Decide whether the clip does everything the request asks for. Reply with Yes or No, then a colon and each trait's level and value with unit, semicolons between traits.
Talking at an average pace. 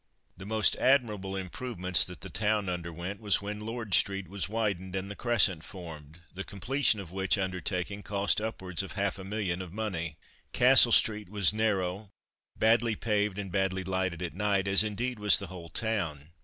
Yes: average, 175 wpm